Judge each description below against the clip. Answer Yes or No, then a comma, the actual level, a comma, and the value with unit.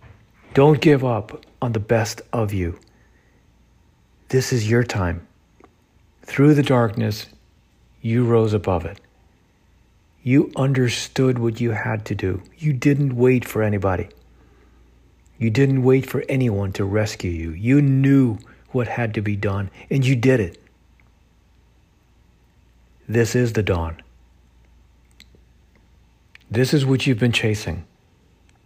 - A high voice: No, low, 110 Hz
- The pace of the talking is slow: Yes, slow, 125 wpm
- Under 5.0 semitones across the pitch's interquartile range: No, wide, 5.4 semitones